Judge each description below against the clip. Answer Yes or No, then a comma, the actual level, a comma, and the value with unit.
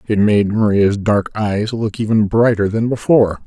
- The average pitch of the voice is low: Yes, low, 105 Hz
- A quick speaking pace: No, average, 175 wpm